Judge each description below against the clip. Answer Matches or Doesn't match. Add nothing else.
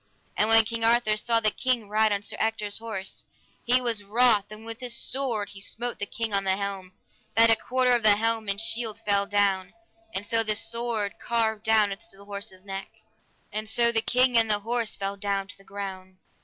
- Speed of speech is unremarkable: Doesn't match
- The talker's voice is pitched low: Doesn't match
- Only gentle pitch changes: Matches